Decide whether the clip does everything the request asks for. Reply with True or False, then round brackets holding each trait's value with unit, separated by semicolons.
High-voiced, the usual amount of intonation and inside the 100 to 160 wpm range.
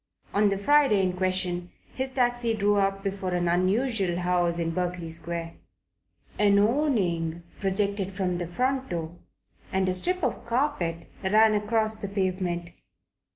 True (195 Hz; 3.6 semitones; 150 wpm)